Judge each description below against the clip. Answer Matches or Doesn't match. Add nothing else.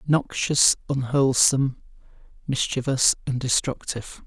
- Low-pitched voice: Matches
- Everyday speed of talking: Doesn't match